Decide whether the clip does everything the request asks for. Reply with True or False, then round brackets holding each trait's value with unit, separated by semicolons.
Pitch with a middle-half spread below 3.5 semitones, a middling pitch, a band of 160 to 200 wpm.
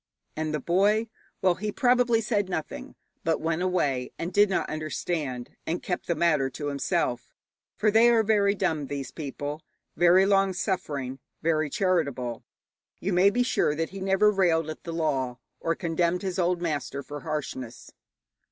False (4.7 semitones; 170 Hz; 165 wpm)